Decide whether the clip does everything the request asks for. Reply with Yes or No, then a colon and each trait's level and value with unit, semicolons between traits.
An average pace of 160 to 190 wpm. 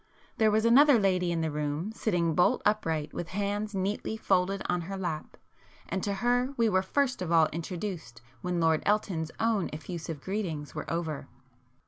Yes: average, 170 wpm